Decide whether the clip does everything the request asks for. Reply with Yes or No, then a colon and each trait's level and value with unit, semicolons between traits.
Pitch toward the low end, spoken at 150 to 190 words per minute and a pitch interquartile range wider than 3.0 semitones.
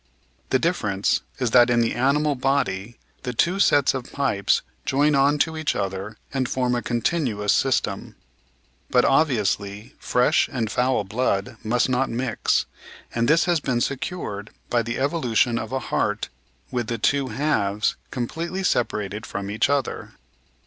Yes: low, 125 Hz; average, 155 wpm; average, 4.1 semitones